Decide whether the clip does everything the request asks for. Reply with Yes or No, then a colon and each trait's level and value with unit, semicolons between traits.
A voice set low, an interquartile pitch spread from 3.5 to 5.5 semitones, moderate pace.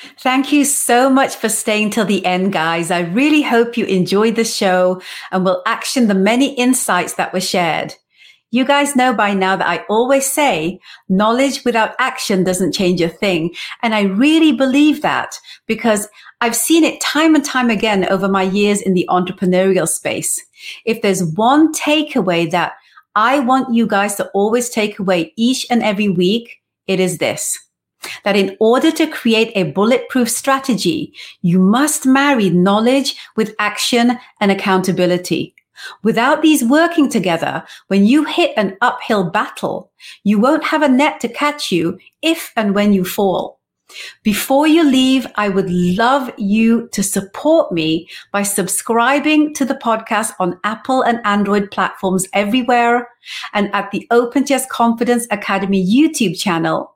No: high, 225 Hz; average, 5.2 semitones; average, 160 wpm